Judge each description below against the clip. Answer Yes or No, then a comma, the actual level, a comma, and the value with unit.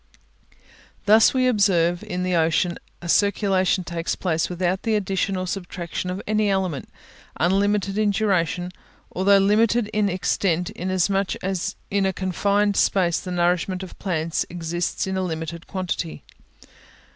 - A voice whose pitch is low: No, medium, 185 Hz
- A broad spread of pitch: No, narrow, 2.4 semitones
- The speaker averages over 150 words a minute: No, average, 140 wpm